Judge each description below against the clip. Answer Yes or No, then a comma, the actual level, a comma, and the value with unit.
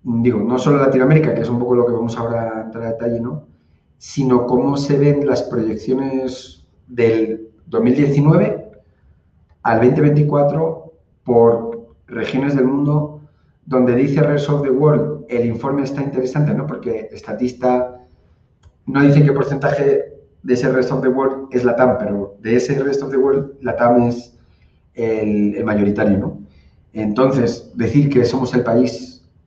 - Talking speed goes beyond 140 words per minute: Yes, average, 155 wpm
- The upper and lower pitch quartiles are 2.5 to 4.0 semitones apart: Yes, average, 3.3 semitones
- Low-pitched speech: Yes, low, 125 Hz